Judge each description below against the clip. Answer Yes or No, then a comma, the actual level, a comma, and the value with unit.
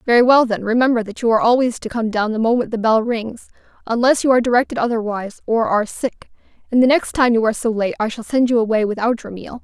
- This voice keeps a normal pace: No, fast, 250 wpm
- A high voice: Yes, high, 230 Hz